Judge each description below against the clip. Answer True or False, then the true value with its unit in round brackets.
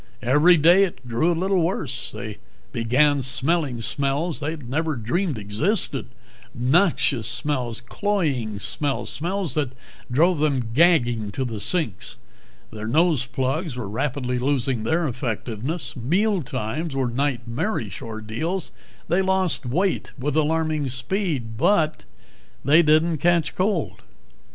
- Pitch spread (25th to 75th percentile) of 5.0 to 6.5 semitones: True (5.6 semitones)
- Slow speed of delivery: True (120 wpm)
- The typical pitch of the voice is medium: True (145 Hz)